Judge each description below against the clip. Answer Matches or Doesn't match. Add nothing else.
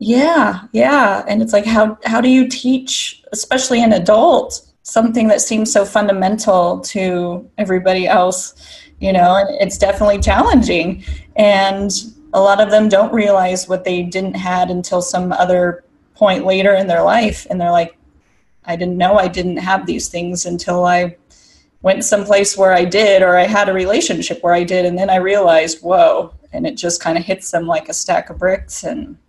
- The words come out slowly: Doesn't match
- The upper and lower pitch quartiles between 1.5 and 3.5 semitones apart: Matches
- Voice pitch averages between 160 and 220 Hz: Matches